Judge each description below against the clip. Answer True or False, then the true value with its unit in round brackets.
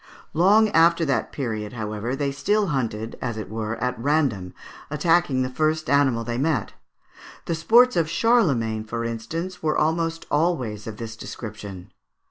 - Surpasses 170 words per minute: False (150 wpm)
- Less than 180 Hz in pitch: True (135 Hz)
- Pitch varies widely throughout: True (6.6 semitones)